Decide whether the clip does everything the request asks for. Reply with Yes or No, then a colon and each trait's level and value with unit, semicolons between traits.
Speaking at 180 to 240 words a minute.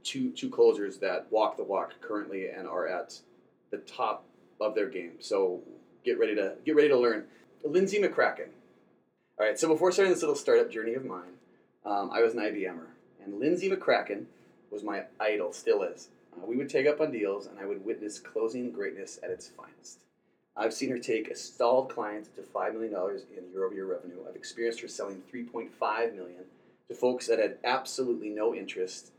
Yes: average, 190 wpm